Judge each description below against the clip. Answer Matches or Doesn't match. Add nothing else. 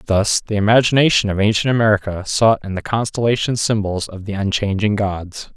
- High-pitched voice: Doesn't match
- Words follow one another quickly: Doesn't match